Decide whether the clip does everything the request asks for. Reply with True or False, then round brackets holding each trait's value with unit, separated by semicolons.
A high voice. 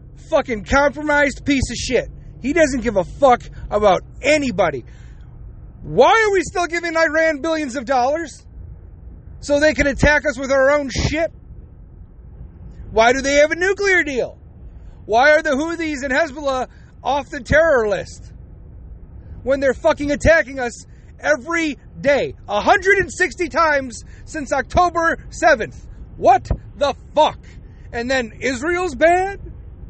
True (295 Hz)